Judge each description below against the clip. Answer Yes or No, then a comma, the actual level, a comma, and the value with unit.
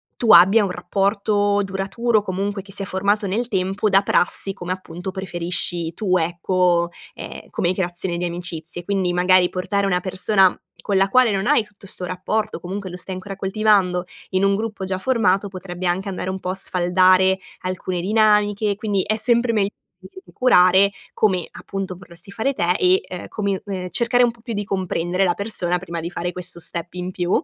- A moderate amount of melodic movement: No, narrow, 2.1 semitones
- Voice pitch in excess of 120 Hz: Yes, high, 190 Hz